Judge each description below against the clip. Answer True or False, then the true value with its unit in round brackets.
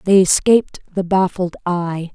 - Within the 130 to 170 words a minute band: True (140 wpm)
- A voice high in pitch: False (180 Hz)